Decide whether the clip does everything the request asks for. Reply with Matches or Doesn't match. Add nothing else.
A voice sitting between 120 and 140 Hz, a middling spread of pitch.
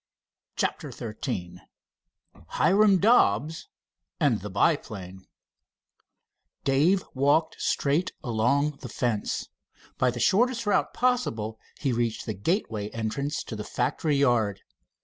Doesn't match